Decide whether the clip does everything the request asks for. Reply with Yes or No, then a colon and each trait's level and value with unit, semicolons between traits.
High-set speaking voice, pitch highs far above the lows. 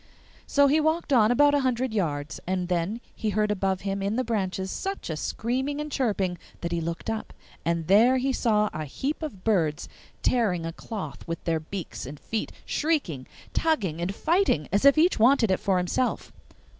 Yes: high, 210 Hz; wide, 6.9 semitones